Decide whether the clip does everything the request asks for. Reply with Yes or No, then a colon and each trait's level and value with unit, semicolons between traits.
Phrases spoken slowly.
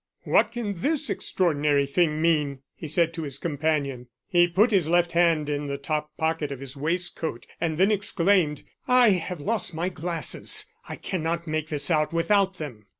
No: average, 175 wpm